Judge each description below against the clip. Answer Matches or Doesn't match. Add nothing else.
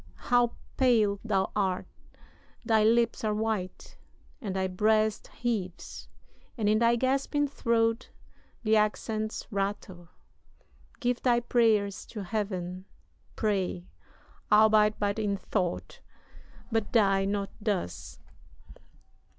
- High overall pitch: Matches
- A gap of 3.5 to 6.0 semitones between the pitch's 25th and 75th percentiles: Doesn't match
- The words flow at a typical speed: Doesn't match